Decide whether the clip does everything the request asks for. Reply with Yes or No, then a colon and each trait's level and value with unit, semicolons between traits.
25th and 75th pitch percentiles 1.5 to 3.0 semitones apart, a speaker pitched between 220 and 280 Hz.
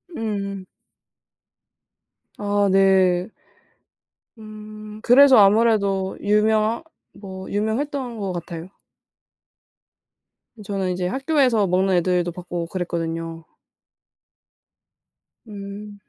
No: average, 2.7 semitones; high, 200 Hz